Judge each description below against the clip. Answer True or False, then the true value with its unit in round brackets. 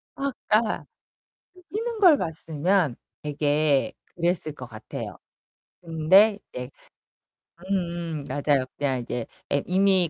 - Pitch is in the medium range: True (165 Hz)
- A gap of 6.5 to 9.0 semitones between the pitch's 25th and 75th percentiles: False (5.4 semitones)